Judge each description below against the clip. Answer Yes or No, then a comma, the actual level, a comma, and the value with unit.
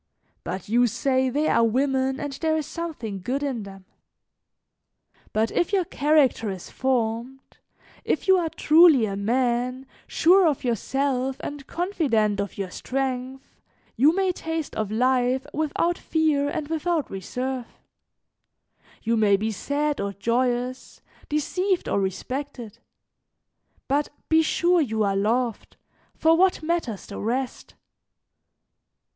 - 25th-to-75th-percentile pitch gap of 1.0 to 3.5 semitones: No, average, 5.2 semitones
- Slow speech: Yes, slow, 130 wpm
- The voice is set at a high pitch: Yes, very high, 260 Hz